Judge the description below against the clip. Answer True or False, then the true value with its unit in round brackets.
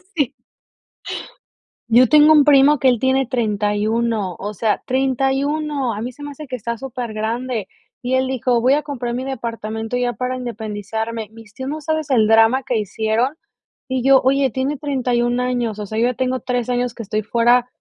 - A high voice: True (245 Hz)